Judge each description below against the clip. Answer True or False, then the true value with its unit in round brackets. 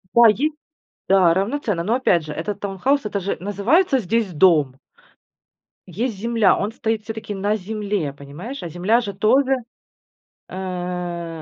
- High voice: True (200 Hz)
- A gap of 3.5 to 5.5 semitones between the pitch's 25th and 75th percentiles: True (4.1 semitones)